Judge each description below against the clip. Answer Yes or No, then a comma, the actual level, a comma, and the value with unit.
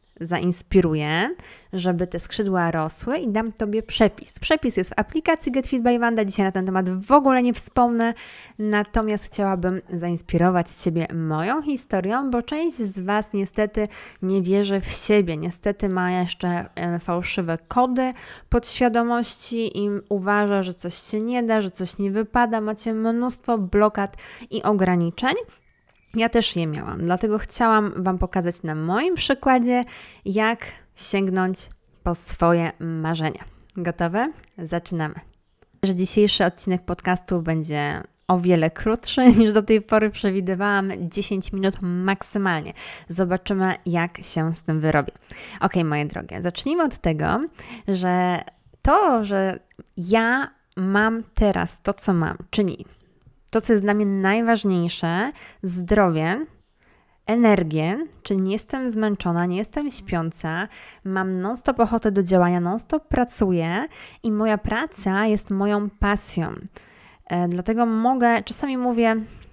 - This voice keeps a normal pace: Yes, average, 130 wpm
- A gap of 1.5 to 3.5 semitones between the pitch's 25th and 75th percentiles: No, average, 4.1 semitones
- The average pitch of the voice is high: Yes, high, 200 Hz